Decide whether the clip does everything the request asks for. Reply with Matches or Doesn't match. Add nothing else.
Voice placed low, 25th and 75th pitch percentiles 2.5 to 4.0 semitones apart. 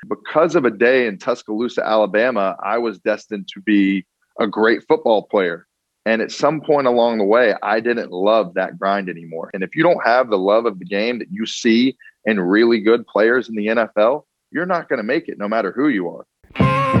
Matches